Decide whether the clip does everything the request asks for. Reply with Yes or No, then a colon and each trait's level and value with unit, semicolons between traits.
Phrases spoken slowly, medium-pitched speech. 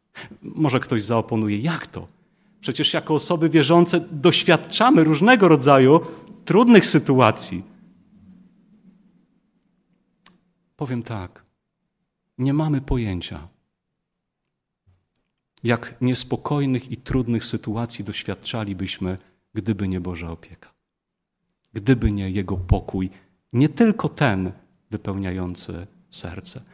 No: slow, 85 wpm; low, 130 Hz